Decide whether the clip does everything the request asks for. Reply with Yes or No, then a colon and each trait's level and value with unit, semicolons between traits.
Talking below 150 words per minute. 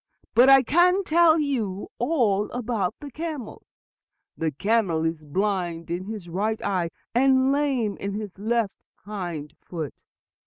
Yes: average, 140 wpm